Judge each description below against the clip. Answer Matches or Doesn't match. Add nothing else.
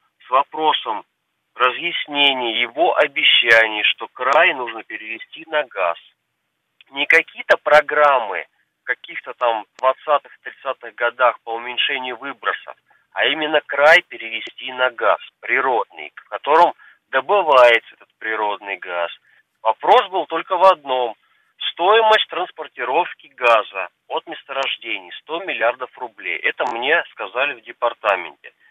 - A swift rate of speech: Doesn't match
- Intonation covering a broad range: Matches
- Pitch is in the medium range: Doesn't match